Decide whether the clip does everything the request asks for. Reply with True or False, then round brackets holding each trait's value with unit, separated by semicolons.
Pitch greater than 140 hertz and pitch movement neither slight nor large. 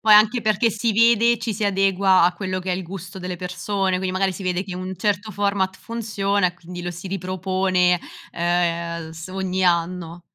False (185 Hz; 2.1 semitones)